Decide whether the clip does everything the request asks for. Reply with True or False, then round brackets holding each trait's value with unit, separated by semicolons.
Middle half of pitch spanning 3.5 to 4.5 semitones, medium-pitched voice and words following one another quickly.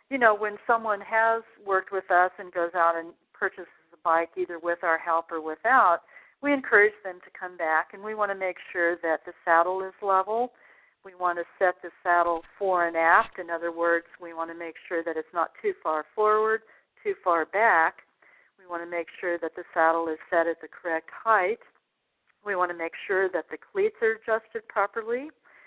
True (4.1 semitones; 180 Hz; 210 wpm)